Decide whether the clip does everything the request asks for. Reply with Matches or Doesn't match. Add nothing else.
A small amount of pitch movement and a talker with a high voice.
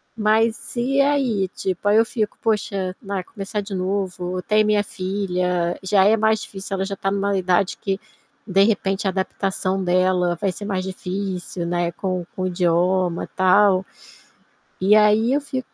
Matches